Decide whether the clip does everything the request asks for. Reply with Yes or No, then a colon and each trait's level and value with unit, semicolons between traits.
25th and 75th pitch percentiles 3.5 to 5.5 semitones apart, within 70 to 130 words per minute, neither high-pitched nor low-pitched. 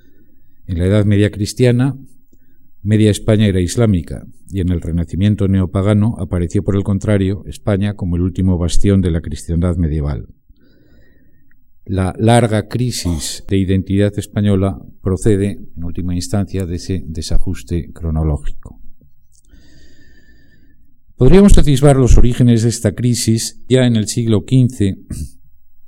No: average, 4.0 semitones; slow, 125 wpm; very low, 95 Hz